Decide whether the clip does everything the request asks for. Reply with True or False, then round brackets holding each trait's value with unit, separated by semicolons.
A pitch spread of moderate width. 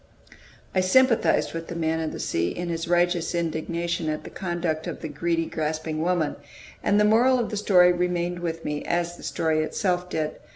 False (2.0 semitones)